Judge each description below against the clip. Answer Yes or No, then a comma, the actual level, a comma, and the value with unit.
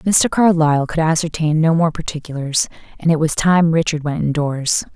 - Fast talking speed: No, average, 170 wpm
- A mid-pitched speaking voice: Yes, medium, 160 Hz